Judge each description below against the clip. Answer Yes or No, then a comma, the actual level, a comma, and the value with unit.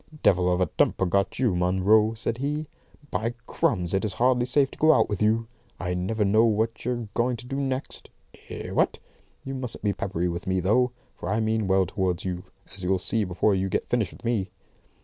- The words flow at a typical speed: No, fast, 210 wpm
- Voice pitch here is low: Yes, low, 105 Hz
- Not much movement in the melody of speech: No, average, 4.3 semitones